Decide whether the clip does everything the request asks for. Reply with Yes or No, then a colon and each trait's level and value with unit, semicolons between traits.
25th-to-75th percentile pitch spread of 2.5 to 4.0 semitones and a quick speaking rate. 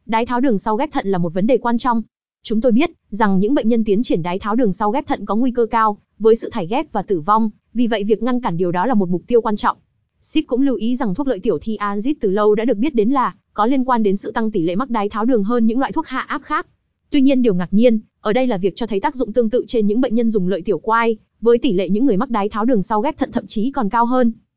Yes: average, 3.3 semitones; fast, 310 wpm